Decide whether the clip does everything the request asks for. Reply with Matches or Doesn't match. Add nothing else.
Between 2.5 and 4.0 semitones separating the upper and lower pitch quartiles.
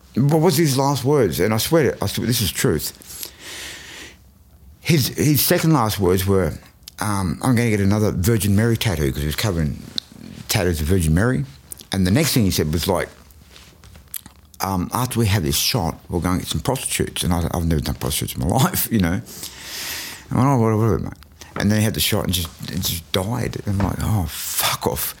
Doesn't match